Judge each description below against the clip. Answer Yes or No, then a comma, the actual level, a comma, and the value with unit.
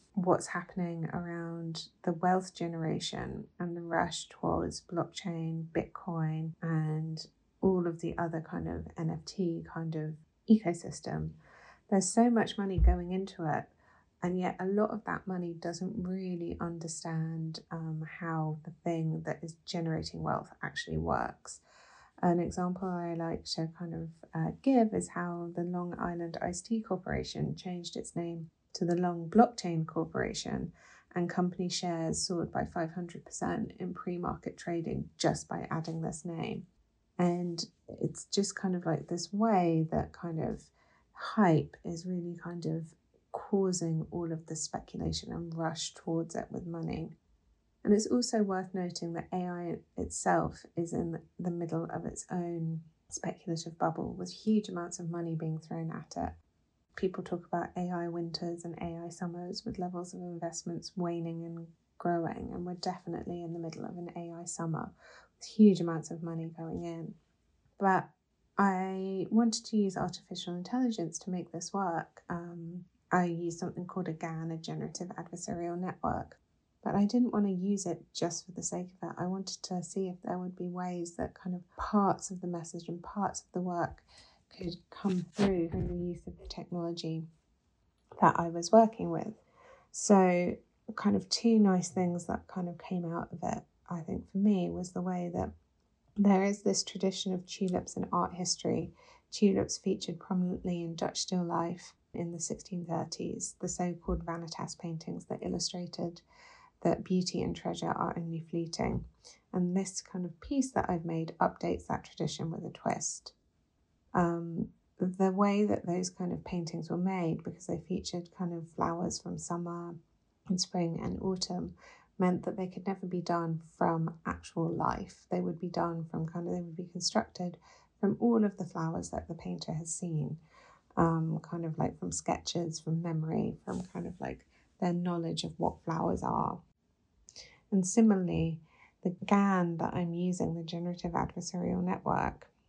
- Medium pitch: Yes, medium, 175 Hz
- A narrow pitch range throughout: Yes, narrow, 2.0 semitones